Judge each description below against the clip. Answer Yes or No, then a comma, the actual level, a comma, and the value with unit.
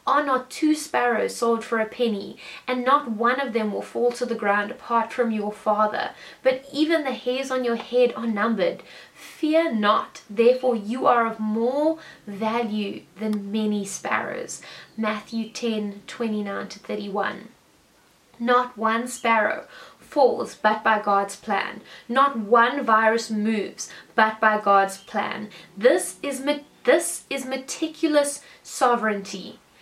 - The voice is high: Yes, high, 230 Hz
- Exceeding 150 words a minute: No, slow, 135 wpm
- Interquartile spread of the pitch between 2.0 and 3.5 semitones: Yes, average, 3.0 semitones